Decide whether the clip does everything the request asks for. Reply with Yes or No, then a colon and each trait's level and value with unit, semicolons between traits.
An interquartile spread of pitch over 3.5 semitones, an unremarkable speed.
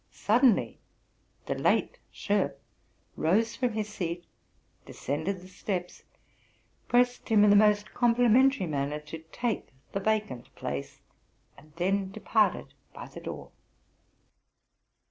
No: average, 4.7 semitones; slow, 115 wpm